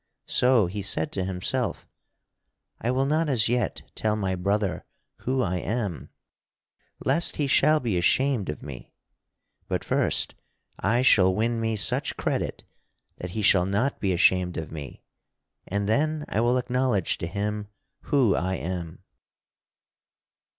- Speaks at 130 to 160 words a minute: Yes, average, 145 wpm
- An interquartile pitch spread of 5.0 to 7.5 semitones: Yes, average, 5.3 semitones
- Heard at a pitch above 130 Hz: No, low, 105 Hz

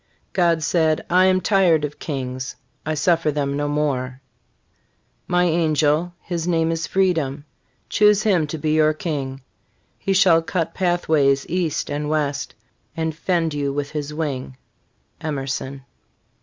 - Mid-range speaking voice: Yes, medium, 155 Hz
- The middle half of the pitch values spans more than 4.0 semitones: No, average, 3.1 semitones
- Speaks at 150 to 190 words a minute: No, average, 140 wpm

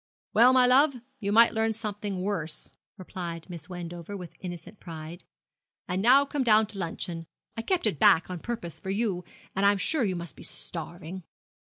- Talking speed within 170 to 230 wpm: Yes, average, 185 wpm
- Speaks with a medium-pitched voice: No, high, 195 Hz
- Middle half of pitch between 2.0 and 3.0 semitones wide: No, average, 4.5 semitones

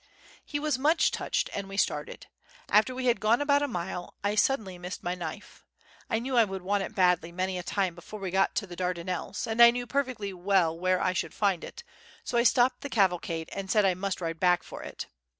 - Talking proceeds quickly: Yes, fast, 225 wpm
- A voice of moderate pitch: No, high, 195 Hz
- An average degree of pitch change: Yes, average, 4.7 semitones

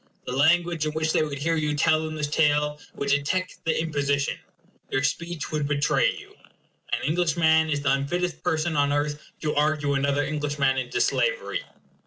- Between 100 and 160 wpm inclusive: No, average, 175 wpm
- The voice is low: No, medium, 150 Hz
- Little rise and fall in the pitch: Yes, narrow, 2.0 semitones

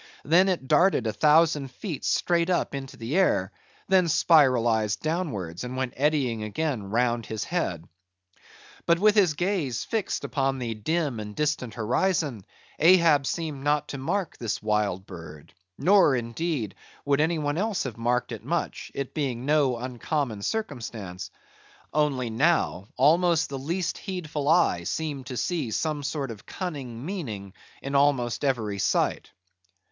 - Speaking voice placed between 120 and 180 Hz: Yes, medium, 140 Hz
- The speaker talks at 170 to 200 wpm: No, average, 150 wpm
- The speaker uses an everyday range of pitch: No, wide, 5.9 semitones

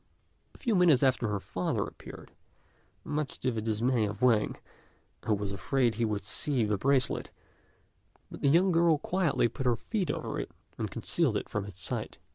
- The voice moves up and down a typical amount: No, wide, 5.7 semitones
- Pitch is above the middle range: No, low, 125 Hz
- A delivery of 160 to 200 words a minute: Yes, average, 180 wpm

